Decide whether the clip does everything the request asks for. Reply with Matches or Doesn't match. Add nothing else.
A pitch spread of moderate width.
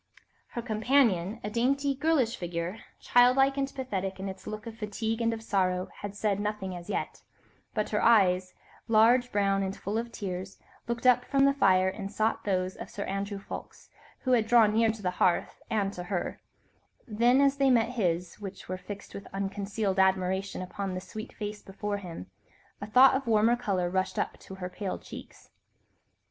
Matches